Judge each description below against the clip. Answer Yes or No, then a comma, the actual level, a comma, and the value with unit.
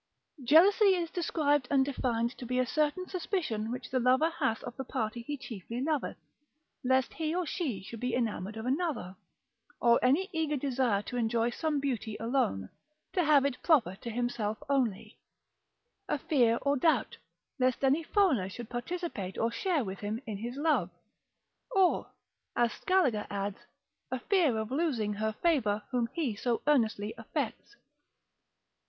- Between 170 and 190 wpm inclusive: No, average, 160 wpm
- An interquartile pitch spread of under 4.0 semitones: No, average, 5.2 semitones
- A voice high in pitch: Yes, very high, 250 Hz